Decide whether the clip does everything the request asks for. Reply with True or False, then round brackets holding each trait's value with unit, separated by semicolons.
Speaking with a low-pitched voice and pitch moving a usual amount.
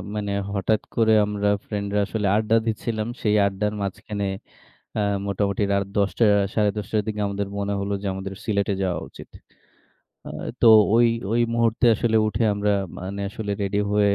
False (105 Hz; 1.5 semitones)